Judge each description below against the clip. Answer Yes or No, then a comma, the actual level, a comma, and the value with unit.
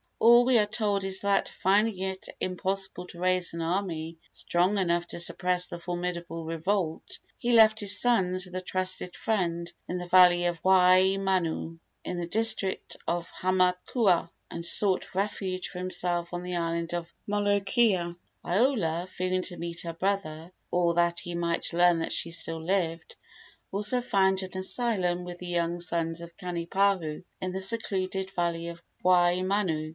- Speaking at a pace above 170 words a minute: No, average, 160 wpm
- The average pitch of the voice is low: No, medium, 180 Hz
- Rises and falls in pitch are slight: Yes, narrow, 2.2 semitones